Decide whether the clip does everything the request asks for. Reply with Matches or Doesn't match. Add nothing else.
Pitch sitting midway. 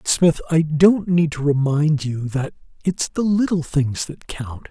Matches